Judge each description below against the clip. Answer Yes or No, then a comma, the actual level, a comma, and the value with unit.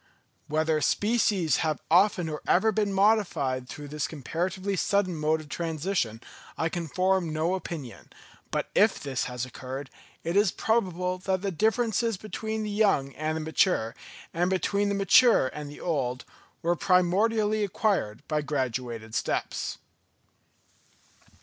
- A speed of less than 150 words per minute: Yes, average, 140 wpm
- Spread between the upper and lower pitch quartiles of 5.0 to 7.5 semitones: Yes, average, 5.3 semitones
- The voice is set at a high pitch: No, medium, 175 Hz